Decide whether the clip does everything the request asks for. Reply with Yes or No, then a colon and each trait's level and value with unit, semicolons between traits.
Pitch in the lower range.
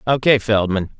Yes: low, 110 Hz